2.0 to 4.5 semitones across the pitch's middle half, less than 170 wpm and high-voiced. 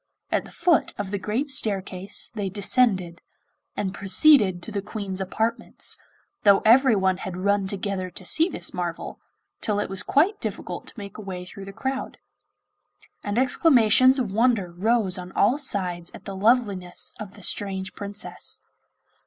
Yes: average, 3.4 semitones; average, 160 wpm; high, 200 Hz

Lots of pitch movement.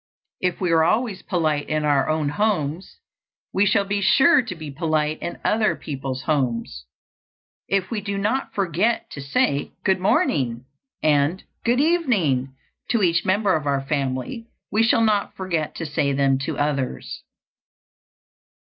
Yes: wide, 6.0 semitones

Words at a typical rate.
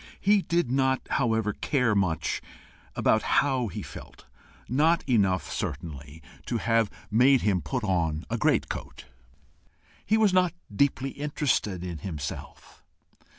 No: slow, 125 wpm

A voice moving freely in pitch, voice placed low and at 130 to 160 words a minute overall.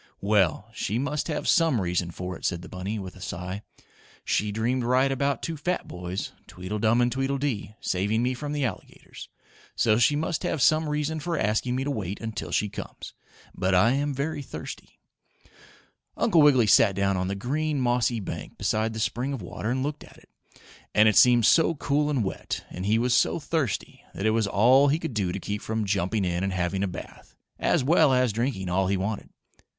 No: wide, 6.0 semitones; low, 115 Hz; fast, 205 wpm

